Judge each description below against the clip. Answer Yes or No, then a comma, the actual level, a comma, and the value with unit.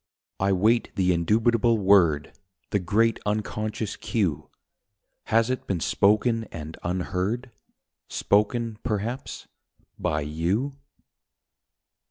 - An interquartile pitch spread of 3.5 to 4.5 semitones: Yes, average, 4.0 semitones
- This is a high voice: No, low, 105 Hz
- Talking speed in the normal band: No, slow, 95 wpm